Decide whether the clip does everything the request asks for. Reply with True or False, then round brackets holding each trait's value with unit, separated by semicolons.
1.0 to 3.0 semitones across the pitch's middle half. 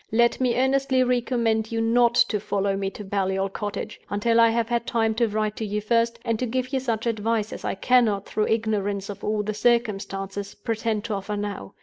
True (2.5 semitones)